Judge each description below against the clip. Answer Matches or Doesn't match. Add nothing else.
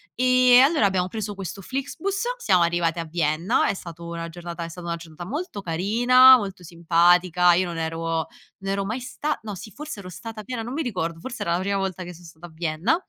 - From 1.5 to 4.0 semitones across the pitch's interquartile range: Doesn't match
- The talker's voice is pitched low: Doesn't match